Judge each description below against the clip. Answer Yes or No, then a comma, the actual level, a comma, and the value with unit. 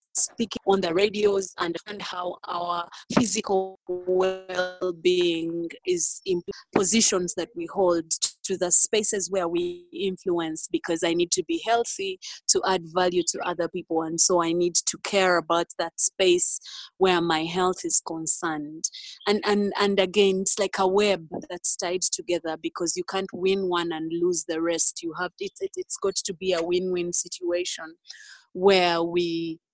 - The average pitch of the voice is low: No, medium, 180 Hz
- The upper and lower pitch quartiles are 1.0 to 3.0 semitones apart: Yes, narrow, 2.6 semitones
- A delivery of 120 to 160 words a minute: No, average, 170 wpm